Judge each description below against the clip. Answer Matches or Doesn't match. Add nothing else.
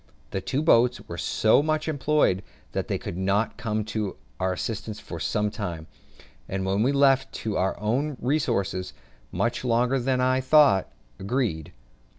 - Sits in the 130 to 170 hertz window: Doesn't match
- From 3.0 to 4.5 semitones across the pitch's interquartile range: Doesn't match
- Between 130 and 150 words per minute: Doesn't match